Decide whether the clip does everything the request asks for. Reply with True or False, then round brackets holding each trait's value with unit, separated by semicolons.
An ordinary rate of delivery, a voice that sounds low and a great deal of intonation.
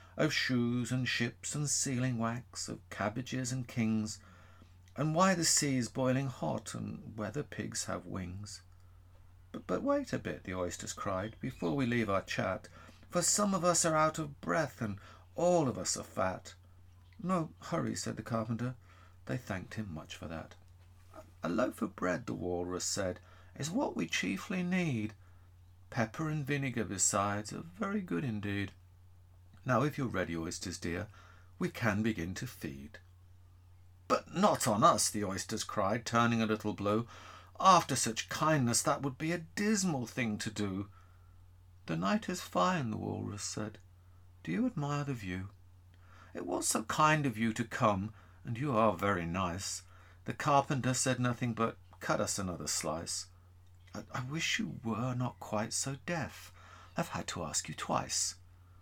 True (165 wpm; 105 Hz; 6.1 semitones)